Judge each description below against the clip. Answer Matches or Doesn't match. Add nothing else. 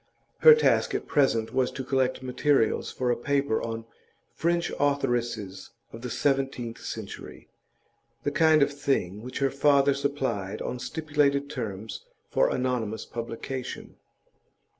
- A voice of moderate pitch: Doesn't match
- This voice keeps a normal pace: Doesn't match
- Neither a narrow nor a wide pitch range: Matches